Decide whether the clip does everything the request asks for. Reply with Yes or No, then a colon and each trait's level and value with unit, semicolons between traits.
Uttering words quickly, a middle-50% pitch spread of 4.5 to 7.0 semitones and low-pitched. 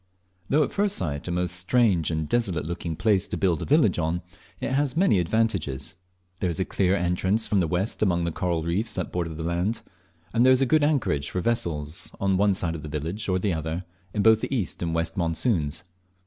Yes: fast, 220 wpm; average, 5.1 semitones; very low, 90 Hz